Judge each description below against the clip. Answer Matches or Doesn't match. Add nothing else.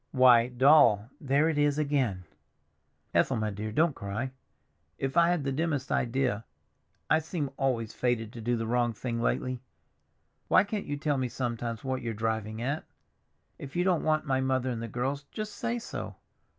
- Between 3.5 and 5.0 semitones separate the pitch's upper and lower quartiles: Matches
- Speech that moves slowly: Doesn't match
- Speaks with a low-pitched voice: Matches